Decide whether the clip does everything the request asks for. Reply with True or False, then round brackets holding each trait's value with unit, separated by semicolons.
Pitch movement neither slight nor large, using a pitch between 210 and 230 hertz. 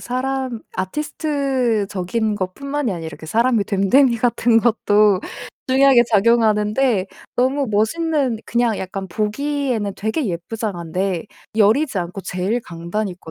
True (4.9 semitones; 220 Hz)